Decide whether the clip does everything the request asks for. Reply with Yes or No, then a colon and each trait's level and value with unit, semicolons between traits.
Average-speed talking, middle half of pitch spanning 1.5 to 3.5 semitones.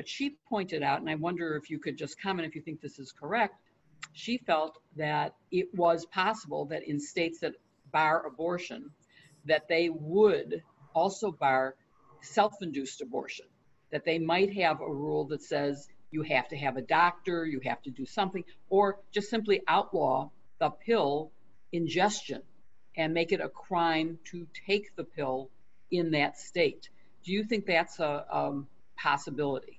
No: average, 165 wpm; average, 4.2 semitones